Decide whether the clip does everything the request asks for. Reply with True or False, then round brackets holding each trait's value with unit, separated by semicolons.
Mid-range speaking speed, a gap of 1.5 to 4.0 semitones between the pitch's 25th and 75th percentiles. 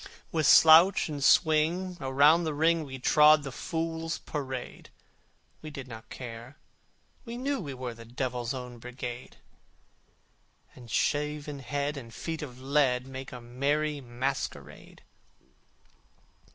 False (125 wpm; 3.7 semitones)